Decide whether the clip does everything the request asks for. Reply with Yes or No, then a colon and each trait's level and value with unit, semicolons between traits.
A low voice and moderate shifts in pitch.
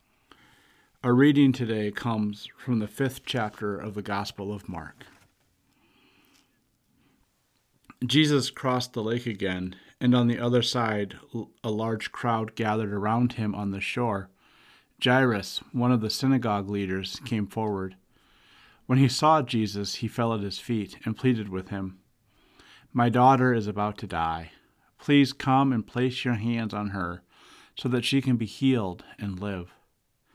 Yes: low, 110 Hz; average, 3.6 semitones